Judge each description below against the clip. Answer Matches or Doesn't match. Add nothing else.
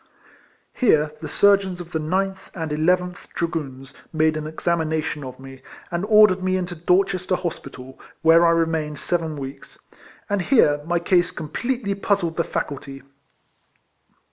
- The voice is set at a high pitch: Doesn't match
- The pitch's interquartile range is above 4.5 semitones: Doesn't match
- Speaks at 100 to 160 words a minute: Matches